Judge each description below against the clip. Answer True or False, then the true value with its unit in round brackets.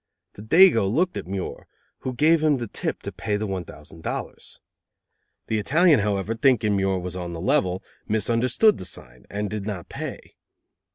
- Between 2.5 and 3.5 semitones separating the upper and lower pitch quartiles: False (5.4 semitones)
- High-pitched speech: False (105 Hz)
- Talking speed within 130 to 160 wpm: False (175 wpm)